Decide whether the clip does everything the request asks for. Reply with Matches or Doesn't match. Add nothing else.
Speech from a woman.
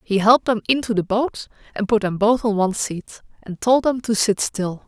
Matches